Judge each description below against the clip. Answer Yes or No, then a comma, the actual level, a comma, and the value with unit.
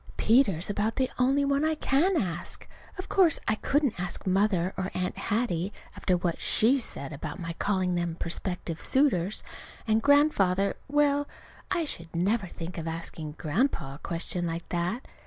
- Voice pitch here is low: No, high, 195 Hz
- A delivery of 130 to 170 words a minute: Yes, average, 160 wpm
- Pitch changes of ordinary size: No, wide, 7.8 semitones